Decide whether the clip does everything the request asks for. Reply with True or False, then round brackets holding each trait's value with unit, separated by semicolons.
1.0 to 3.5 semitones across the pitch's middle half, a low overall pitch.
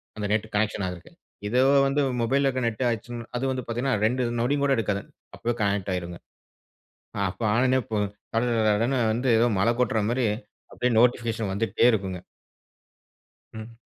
True (2.9 semitones; 115 Hz)